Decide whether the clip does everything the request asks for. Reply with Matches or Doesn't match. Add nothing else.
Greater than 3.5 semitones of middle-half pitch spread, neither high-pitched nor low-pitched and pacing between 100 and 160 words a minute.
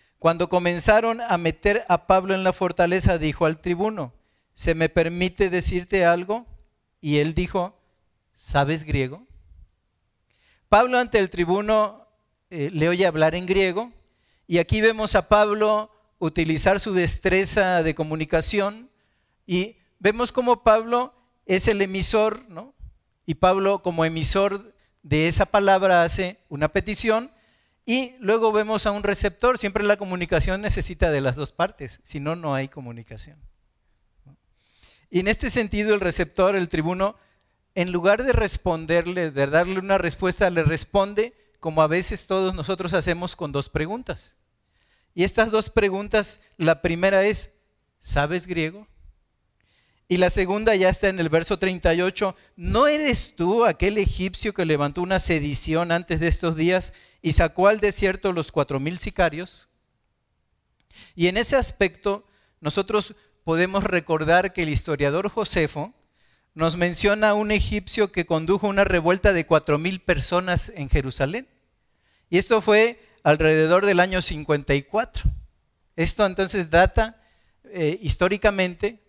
Matches